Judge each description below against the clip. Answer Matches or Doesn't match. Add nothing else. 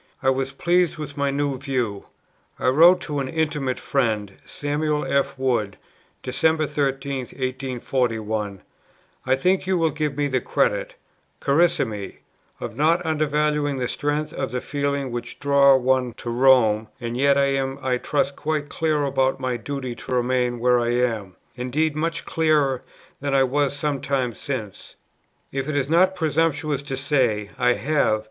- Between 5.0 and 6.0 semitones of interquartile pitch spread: Doesn't match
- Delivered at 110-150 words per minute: Doesn't match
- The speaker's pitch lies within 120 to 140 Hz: Matches